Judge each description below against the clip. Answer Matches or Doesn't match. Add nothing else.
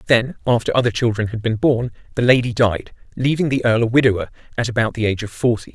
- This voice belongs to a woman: Doesn't match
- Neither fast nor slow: Doesn't match